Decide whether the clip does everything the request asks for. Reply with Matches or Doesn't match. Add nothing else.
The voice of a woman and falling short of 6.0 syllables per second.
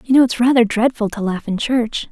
Matches